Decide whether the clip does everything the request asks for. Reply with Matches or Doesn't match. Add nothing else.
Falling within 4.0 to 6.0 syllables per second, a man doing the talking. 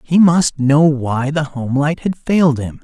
Matches